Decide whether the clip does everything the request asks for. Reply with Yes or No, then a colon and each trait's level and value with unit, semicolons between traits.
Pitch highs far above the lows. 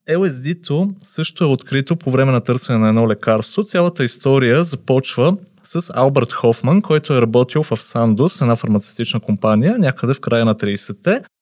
Yes: wide, 6.2 semitones